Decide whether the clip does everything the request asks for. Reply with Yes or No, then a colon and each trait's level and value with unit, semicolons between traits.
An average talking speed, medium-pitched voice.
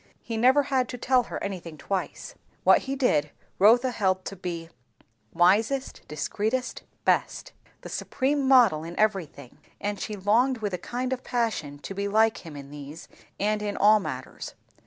No: average, 165 wpm; high, 210 Hz